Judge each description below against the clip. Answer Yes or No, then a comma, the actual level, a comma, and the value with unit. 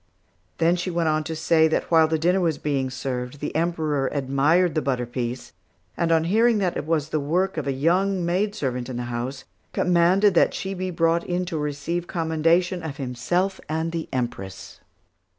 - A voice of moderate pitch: Yes, medium, 160 Hz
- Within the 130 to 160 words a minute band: No, average, 185 wpm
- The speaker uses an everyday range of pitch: Yes, average, 4.2 semitones